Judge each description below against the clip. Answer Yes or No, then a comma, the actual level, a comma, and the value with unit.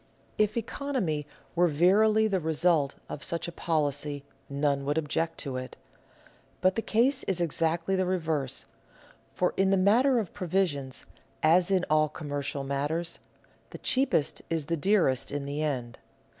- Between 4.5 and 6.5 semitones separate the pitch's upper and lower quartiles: Yes, average, 4.8 semitones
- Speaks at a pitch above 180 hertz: No, medium, 165 Hz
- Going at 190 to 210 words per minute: No, average, 150 wpm